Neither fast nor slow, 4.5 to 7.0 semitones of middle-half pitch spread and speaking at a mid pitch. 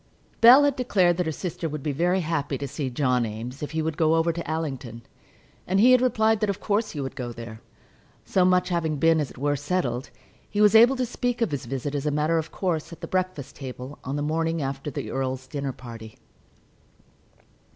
No: fast, 220 wpm; wide, 5.4 semitones; medium, 155 Hz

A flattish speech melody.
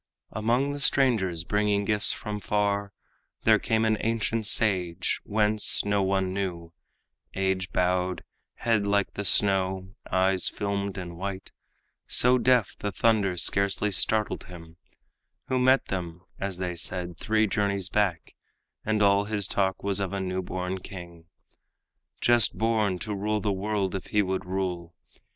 Yes: narrow, 2.3 semitones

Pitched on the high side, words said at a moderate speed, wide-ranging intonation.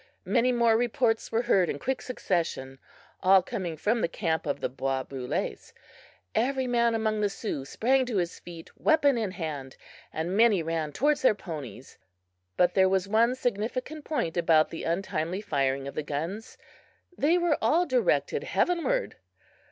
Yes: high, 200 Hz; average, 160 wpm; wide, 7.3 semitones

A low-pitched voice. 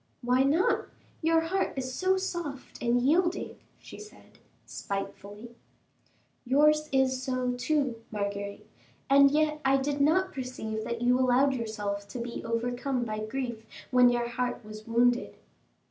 No: very high, 250 Hz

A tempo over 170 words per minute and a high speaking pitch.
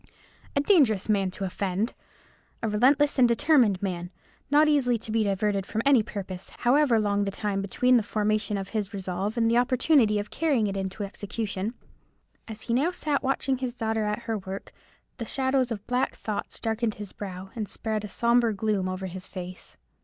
Yes: average, 185 wpm; high, 215 Hz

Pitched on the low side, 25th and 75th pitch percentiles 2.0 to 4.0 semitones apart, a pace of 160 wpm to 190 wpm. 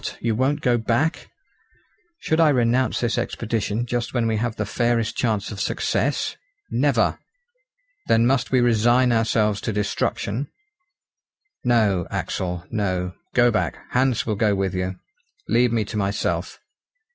No: low, 115 Hz; average, 2.8 semitones; average, 140 wpm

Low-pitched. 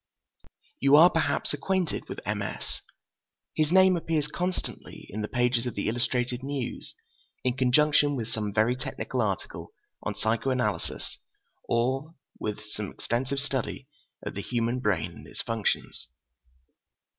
Yes: low, 125 Hz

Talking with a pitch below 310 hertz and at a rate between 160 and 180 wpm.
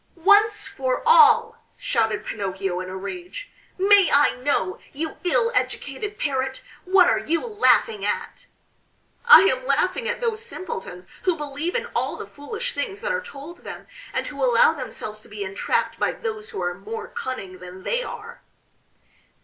No: very high, 360 Hz; average, 165 wpm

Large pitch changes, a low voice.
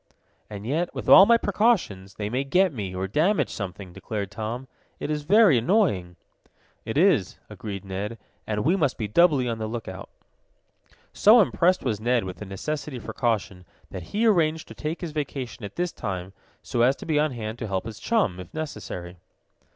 Yes: wide, 7.9 semitones; low, 120 Hz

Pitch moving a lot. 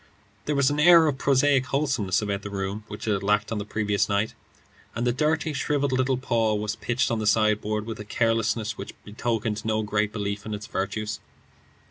No: average, 3.7 semitones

